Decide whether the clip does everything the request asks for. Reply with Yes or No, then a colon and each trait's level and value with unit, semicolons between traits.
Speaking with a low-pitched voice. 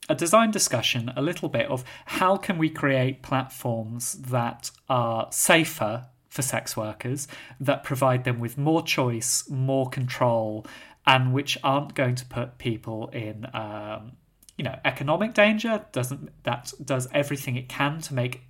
Yes: low, 130 Hz